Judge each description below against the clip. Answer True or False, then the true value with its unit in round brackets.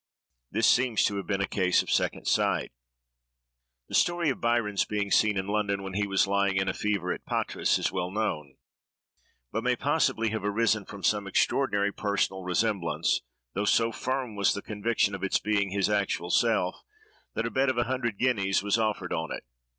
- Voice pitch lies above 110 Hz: False (100 Hz)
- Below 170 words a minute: False (190 wpm)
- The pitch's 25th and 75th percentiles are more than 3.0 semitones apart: False (2.4 semitones)